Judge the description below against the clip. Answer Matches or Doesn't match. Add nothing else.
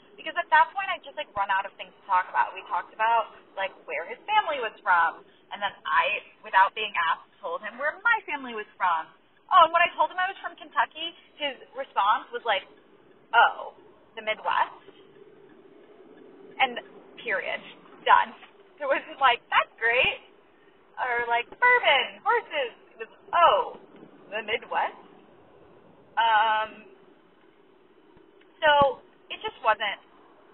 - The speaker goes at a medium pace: Matches